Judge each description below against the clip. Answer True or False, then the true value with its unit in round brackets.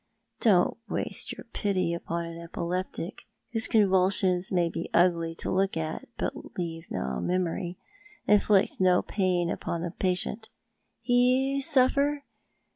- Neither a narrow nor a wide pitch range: True (3.7 semitones)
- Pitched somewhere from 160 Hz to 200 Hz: True (185 Hz)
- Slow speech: True (125 wpm)